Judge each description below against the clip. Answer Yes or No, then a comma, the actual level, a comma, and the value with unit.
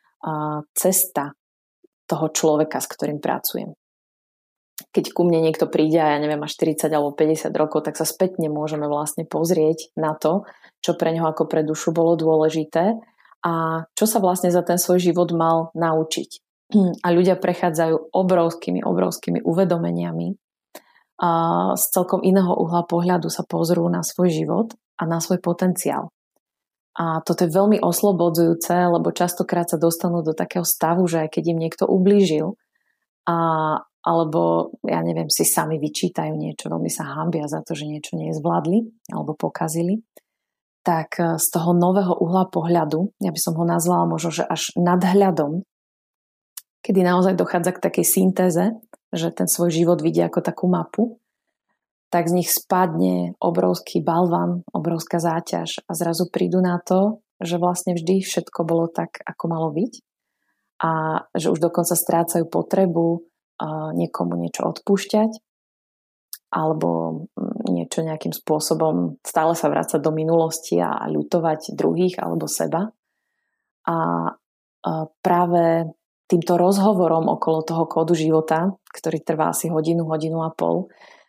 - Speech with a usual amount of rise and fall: No, narrow, 2.3 semitones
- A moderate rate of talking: Yes, average, 140 wpm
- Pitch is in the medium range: Yes, medium, 170 Hz